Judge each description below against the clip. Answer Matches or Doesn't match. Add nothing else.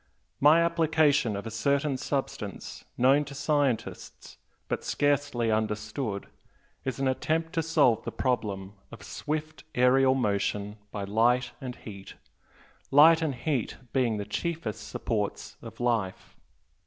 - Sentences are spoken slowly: Matches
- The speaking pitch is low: Matches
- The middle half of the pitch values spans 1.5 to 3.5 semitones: Doesn't match